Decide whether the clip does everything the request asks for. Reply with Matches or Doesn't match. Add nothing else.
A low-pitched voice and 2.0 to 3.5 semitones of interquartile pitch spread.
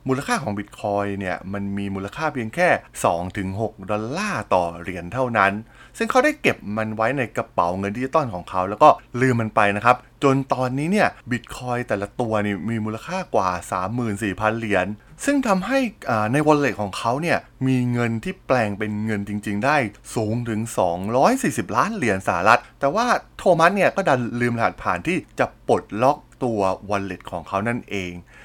Doesn't match